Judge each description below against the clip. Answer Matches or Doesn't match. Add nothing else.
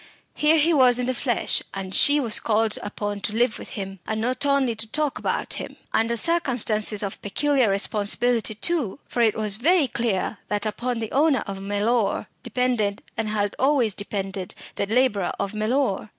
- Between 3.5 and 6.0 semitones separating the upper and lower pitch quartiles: Matches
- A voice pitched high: Matches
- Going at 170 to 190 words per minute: Matches